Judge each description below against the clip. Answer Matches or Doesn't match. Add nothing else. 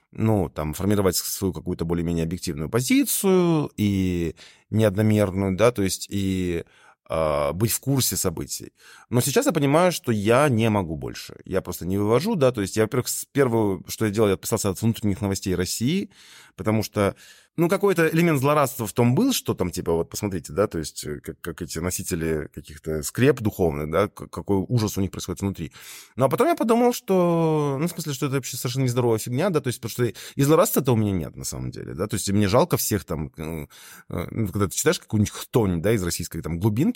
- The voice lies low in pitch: Matches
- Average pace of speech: Doesn't match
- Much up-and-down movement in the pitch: Matches